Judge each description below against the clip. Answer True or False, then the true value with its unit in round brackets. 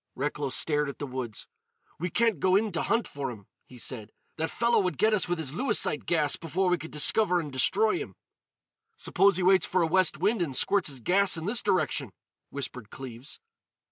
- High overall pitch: False (165 Hz)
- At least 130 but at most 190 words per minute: False (205 wpm)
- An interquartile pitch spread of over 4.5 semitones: True (5.6 semitones)